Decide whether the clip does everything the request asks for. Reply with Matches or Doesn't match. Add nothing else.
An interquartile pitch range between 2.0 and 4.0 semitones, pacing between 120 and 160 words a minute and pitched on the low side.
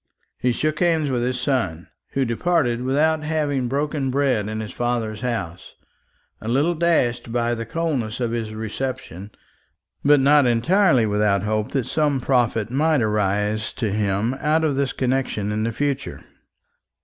Doesn't match